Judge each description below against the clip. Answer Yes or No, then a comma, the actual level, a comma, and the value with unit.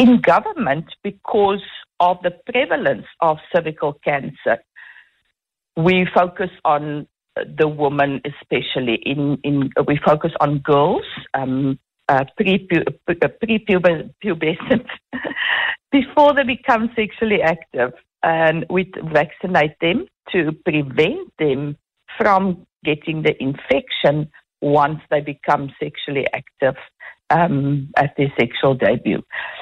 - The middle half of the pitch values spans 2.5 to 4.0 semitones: No, average, 4.9 semitones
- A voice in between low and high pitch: Yes, medium, 160 Hz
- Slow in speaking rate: Yes, slow, 105 wpm